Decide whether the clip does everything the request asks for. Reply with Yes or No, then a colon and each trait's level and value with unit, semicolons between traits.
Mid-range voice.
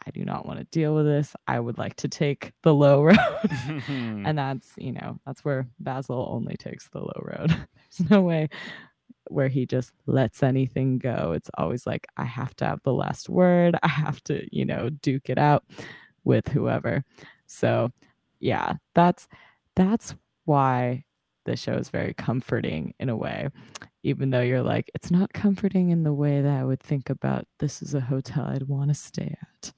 Yes: medium, 145 Hz